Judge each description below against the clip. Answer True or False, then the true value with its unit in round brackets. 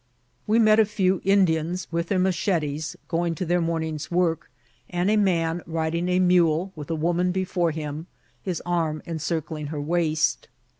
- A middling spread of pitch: False (2.3 semitones)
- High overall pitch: False (170 Hz)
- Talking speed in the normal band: True (165 wpm)